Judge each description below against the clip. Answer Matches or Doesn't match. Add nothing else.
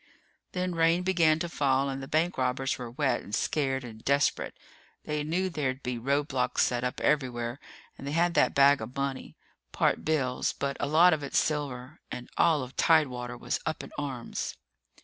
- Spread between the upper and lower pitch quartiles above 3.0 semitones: Matches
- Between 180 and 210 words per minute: Matches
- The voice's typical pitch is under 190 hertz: Matches